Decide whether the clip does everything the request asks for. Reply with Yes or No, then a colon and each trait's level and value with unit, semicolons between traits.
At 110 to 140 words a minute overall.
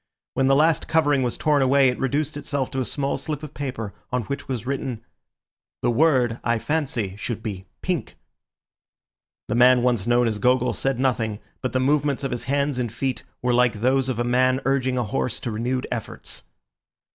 No: average, 190 wpm